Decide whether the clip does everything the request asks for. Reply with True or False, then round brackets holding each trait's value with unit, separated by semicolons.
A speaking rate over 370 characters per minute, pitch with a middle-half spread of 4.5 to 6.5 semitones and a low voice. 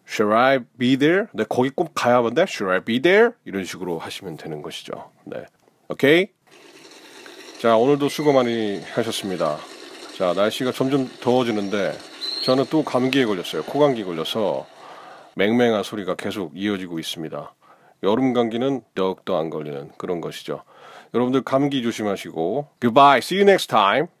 True (395 characters per minute; 5.2 semitones; 125 Hz)